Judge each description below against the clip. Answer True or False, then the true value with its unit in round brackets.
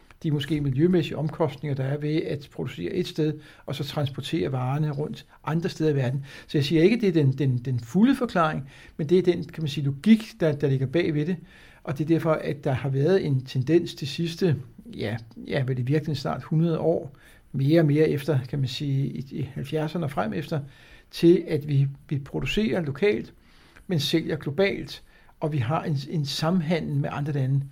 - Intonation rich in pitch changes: False (3.2 semitones)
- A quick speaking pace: False (210 wpm)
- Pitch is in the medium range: True (155 Hz)